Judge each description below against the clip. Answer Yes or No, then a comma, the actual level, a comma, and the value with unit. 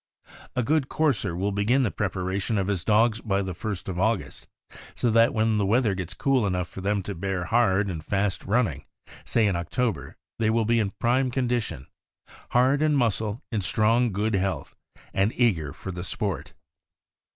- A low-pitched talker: Yes, low, 105 Hz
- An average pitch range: Yes, average, 3.7 semitones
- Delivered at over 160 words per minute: Yes, average, 185 wpm